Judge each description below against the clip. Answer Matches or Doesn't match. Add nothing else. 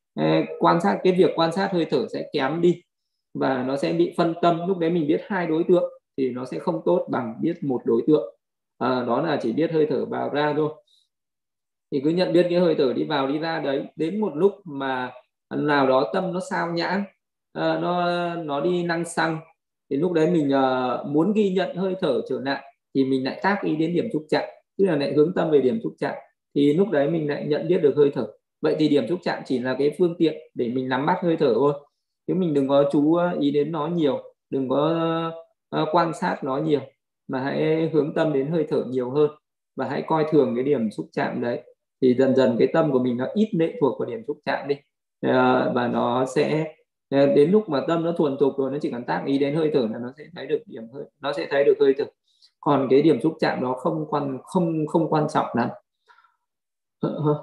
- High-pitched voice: Doesn't match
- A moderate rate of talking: Matches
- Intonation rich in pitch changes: Doesn't match